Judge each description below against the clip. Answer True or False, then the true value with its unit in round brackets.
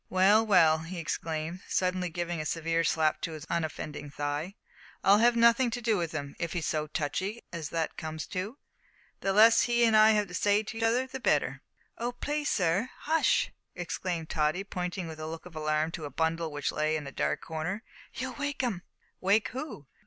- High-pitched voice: False (175 Hz)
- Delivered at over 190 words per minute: True (205 wpm)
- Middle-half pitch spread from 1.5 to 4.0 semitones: False (5.6 semitones)